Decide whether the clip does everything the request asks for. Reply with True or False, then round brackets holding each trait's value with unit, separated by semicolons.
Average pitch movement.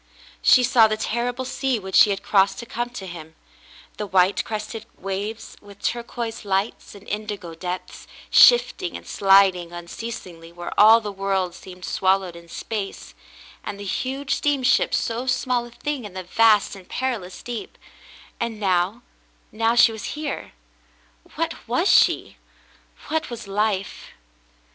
True (3.8 semitones)